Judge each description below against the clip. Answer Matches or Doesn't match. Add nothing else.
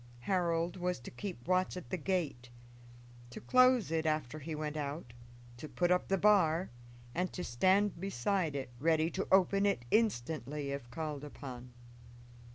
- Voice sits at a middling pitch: Matches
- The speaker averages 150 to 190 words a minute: Matches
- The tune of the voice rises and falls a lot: Doesn't match